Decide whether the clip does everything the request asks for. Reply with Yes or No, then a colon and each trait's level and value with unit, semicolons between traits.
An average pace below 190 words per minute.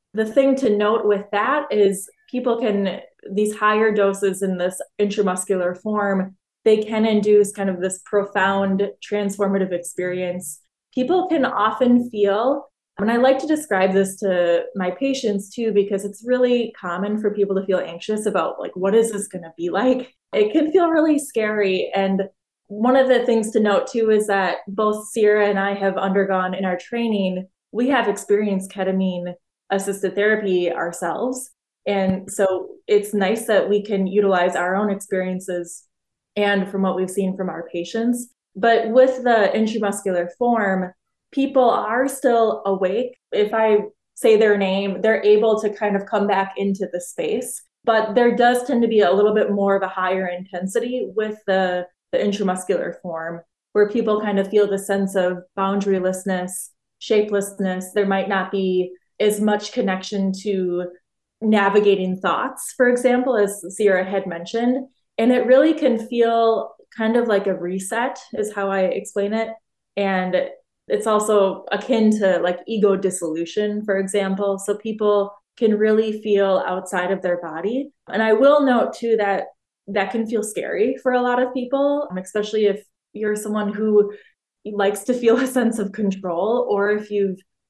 Yes: average, 165 wpm